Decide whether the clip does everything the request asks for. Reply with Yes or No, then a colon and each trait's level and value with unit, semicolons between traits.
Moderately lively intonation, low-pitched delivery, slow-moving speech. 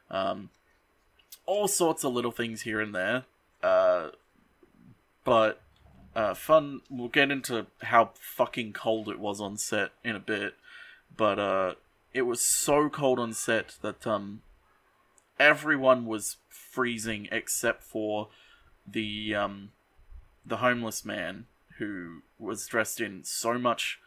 No: wide, 5.8 semitones; low, 120 Hz; slow, 130 wpm